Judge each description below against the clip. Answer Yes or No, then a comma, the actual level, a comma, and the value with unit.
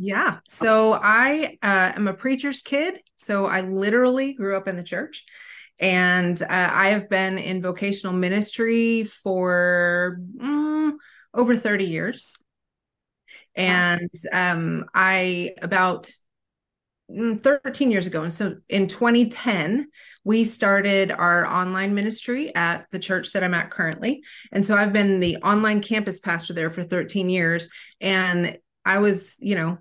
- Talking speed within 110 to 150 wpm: Yes, average, 140 wpm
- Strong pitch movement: No, average, 3.7 semitones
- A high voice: Yes, high, 195 Hz